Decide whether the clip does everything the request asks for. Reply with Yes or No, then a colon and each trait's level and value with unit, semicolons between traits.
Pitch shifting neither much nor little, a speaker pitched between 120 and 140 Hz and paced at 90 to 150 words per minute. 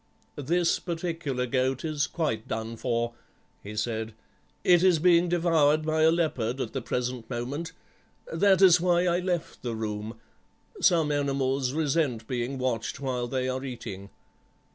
No: wide, 5.7 semitones; low, 135 Hz; average, 145 wpm